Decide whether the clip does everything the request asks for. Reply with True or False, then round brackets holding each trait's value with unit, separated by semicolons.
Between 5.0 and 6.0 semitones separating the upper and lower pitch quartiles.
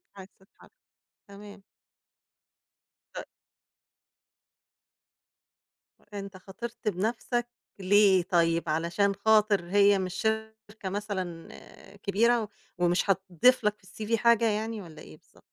False (2.9 semitones)